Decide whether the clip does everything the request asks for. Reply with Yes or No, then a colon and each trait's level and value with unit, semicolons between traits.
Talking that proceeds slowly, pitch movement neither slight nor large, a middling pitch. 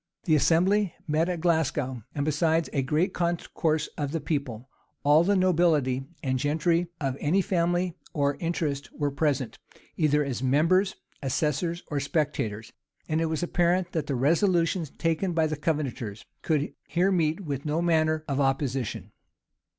No: average, 155 wpm; average, 3.3 semitones; medium, 155 Hz